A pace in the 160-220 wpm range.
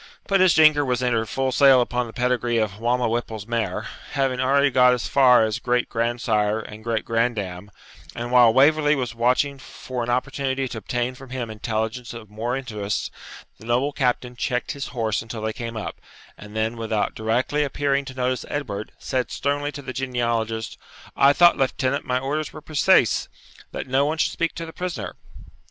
Yes: average, 185 wpm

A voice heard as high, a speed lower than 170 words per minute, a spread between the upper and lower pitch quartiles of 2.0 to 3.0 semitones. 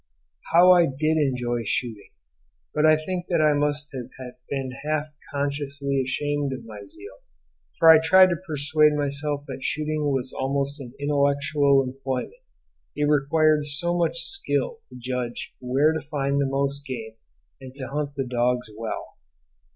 No: medium, 140 Hz; average, 150 wpm; narrow, 2.6 semitones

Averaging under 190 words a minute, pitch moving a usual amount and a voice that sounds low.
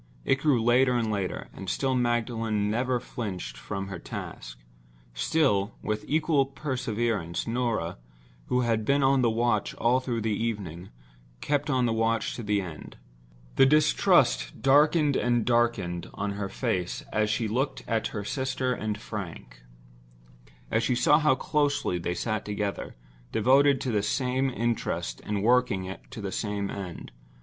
Yes: average, 150 wpm; average, 4.4 semitones; low, 115 Hz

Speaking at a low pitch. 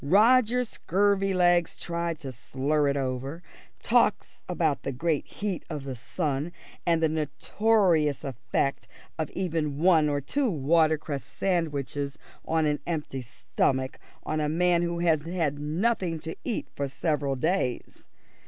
No: medium, 160 Hz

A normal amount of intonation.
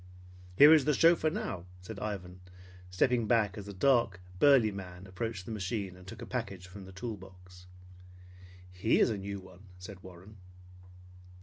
Yes: average, 3.6 semitones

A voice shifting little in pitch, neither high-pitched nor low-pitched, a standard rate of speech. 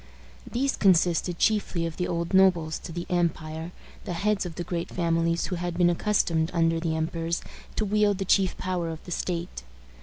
Yes: narrow, 2.0 semitones; medium, 175 Hz; average, 185 wpm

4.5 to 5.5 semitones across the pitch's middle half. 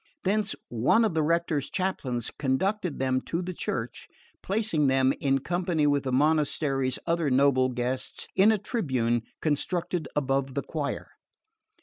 Yes: average, 5.0 semitones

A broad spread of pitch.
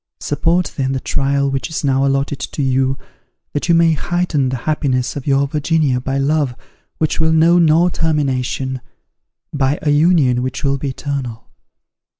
No: average, 3.0 semitones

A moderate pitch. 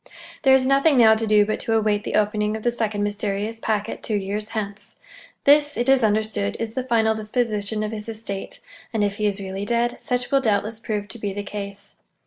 No: high, 215 Hz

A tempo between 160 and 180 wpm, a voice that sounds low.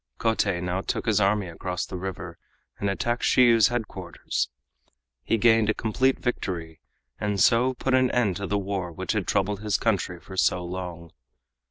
Yes: average, 170 wpm; low, 100 Hz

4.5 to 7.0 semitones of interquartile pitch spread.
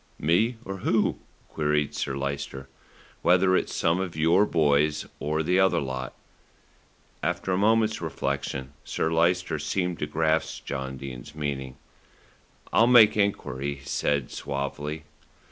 Yes: average, 4.8 semitones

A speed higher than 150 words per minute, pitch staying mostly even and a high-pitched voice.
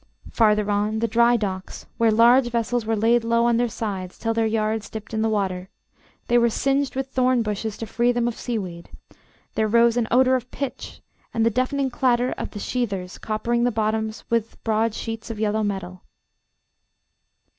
Yes: average, 190 wpm; narrow, 2.0 semitones; high, 225 Hz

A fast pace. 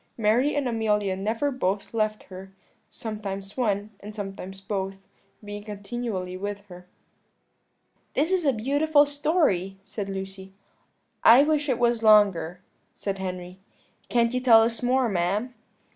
No: slow, 135 wpm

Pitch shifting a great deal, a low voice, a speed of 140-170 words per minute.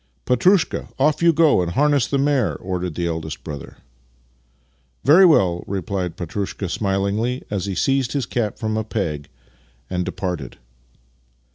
Yes: wide, 7.4 semitones; low, 100 Hz; average, 150 wpm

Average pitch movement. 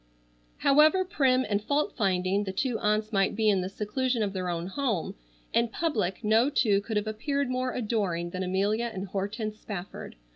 Yes: average, 4.5 semitones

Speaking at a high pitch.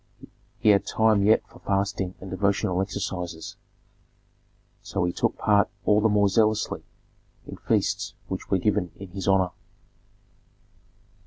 No: low, 100 Hz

